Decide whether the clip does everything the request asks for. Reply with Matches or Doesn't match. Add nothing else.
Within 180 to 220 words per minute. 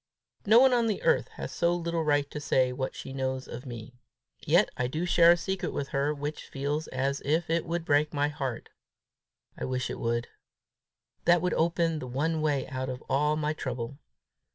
Matches